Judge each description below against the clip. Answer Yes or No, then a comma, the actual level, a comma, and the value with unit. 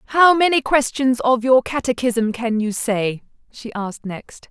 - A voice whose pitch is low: No, high, 245 Hz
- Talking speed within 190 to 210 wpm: No, average, 160 wpm